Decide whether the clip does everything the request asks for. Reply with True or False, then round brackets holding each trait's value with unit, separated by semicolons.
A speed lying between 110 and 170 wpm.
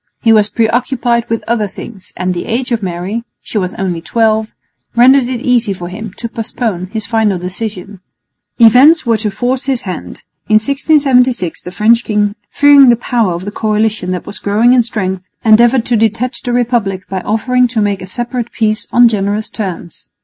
False (185 wpm)